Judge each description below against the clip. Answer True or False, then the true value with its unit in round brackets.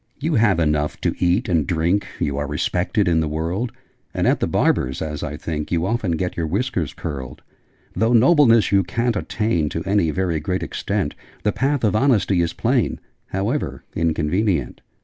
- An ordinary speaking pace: True (175 wpm)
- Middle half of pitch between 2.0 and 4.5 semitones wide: False (5.5 semitones)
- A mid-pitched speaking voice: False (90 Hz)